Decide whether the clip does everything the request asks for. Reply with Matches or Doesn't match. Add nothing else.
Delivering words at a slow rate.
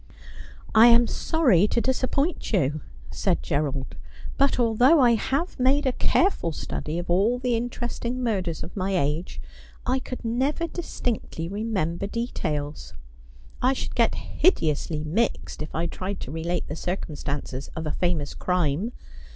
Doesn't match